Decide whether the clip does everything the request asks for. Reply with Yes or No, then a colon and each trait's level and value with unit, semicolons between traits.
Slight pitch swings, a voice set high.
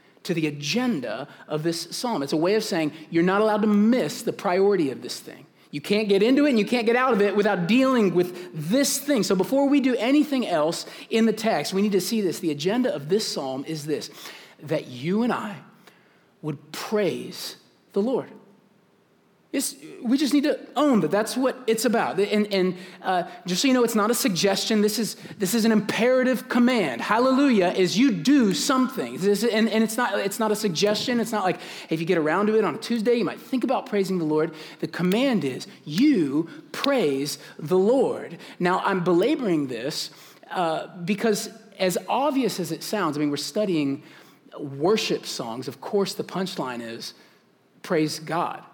No: wide, 5.4 semitones; high, 210 Hz